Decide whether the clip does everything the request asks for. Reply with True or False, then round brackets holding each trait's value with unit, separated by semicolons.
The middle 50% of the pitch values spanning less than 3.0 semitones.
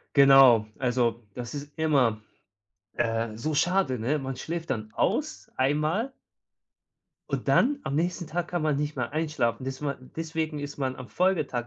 False (4.2 semitones)